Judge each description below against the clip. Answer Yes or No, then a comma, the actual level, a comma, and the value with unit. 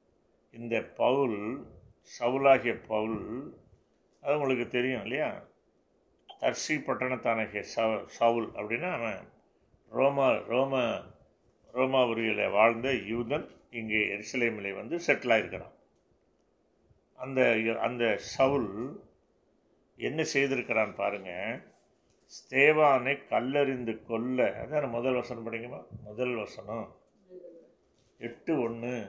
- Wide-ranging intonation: No, average, 2.8 semitones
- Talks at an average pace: Yes, average, 85 wpm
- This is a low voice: Yes, low, 120 Hz